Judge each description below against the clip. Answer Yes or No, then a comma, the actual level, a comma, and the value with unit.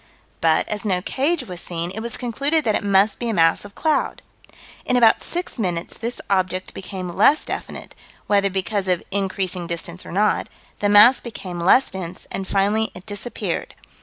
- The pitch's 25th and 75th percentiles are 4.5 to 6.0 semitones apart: No, average, 3.7 semitones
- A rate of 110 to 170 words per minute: No, average, 180 wpm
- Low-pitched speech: No, high, 200 Hz